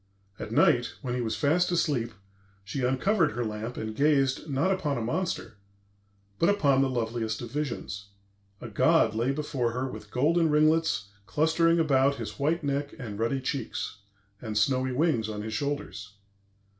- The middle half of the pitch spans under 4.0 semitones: No, average, 5.1 semitones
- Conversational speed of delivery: Yes, average, 160 wpm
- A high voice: No, low, 135 Hz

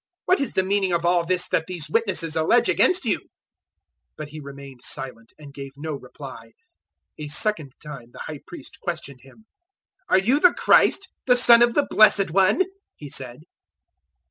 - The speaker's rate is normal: Yes, average, 175 wpm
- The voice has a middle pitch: Yes, medium, 170 Hz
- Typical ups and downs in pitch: No, wide, 7.0 semitones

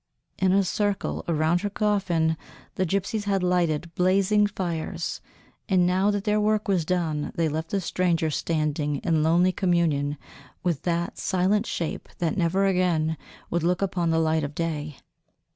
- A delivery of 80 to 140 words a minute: No, average, 160 wpm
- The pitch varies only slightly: No, average, 3.3 semitones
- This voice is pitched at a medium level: Yes, medium, 175 Hz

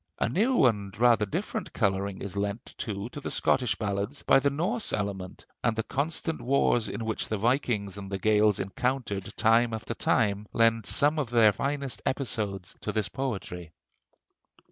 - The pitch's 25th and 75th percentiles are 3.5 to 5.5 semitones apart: Yes, average, 4.4 semitones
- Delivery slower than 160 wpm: No, average, 165 wpm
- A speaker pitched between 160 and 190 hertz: No, low, 110 Hz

